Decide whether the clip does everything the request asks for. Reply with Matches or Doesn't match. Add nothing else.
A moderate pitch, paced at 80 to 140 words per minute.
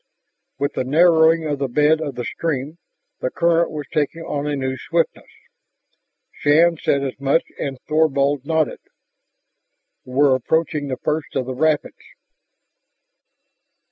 Matches